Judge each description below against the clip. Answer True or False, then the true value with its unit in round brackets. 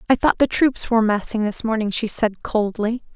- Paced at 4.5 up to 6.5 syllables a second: True (5.2 syllables/s)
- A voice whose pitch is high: True (220 Hz)